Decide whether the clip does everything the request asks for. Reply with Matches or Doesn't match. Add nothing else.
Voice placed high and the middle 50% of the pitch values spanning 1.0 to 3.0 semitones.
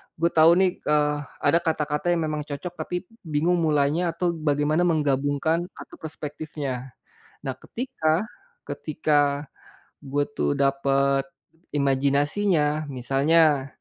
Doesn't match